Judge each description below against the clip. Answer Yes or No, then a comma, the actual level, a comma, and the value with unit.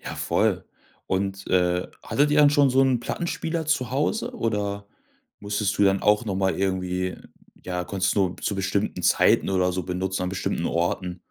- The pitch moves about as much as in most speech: Yes, average, 4.8 semitones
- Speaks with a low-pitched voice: Yes, very low, 95 Hz